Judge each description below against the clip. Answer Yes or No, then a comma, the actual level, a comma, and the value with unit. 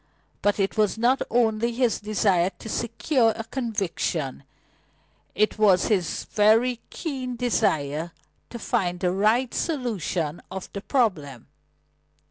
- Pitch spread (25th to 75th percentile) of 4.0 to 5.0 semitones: Yes, average, 4.7 semitones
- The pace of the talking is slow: Yes, slow, 120 wpm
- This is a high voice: Yes, high, 215 Hz